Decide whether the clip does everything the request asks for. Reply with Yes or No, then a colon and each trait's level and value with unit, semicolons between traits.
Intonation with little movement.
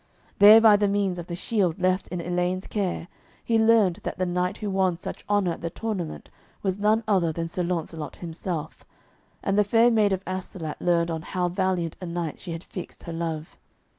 No: average, 3.0 semitones